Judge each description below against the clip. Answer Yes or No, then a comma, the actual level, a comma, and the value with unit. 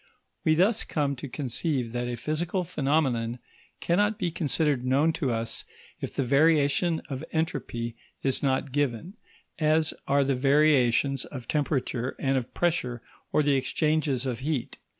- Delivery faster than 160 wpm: No, average, 150 wpm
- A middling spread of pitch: Yes, average, 3.7 semitones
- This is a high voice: No, medium, 140 Hz